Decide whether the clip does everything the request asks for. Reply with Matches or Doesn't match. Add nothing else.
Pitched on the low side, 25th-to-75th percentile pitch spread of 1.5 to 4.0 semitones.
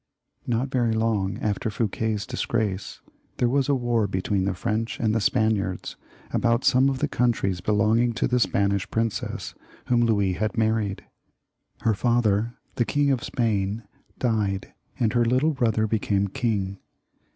Matches